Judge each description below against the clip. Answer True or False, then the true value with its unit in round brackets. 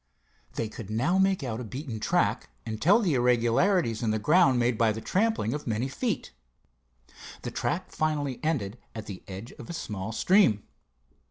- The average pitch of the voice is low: True (120 Hz)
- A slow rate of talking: False (175 wpm)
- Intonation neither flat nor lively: False (6.5 semitones)